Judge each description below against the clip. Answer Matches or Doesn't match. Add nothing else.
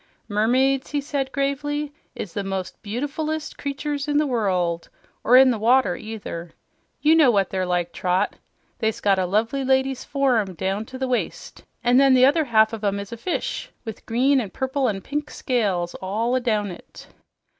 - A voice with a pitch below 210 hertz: Doesn't match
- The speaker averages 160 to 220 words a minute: Matches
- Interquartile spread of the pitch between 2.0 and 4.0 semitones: Doesn't match